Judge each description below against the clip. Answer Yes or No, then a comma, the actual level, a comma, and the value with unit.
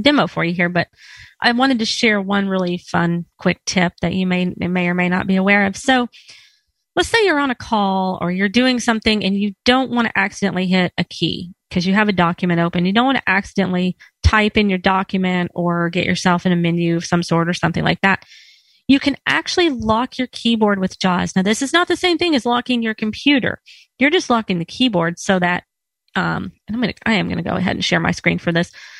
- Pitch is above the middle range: Yes, high, 195 Hz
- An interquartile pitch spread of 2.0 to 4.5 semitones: No, average, 5.3 semitones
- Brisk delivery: Yes, fast, 240 wpm